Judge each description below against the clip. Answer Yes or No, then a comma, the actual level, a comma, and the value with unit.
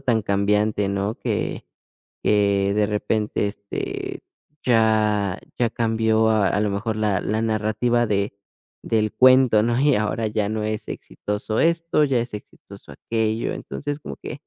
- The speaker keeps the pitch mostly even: Yes, narrow, 1.9 semitones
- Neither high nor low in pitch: No, low, 110 Hz